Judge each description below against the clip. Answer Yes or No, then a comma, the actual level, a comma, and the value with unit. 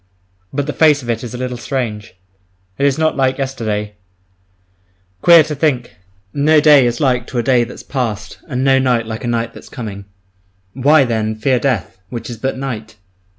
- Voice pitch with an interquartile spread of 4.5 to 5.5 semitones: No, average, 3.2 semitones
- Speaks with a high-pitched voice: No, low, 125 Hz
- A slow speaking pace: No, average, 190 wpm